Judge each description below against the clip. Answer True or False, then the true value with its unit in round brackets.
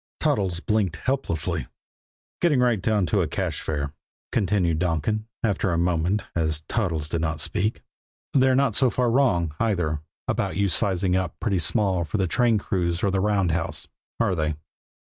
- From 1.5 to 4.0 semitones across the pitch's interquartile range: False (4.5 semitones)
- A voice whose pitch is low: True (95 Hz)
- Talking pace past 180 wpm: False (165 wpm)